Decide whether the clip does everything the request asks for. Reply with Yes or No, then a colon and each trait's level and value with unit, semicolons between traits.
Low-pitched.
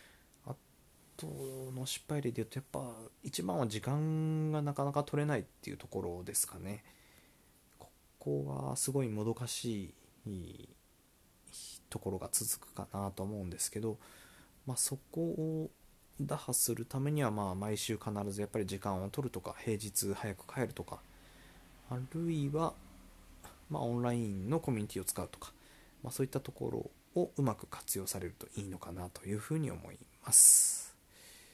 Yes: low, 110 Hz